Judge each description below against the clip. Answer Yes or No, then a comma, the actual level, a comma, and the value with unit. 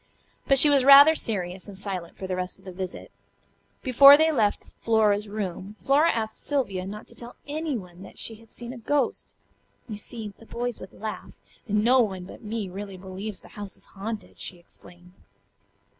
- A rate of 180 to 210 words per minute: Yes, average, 190 wpm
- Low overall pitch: No, high, 210 Hz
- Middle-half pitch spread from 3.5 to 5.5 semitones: Yes, average, 4.4 semitones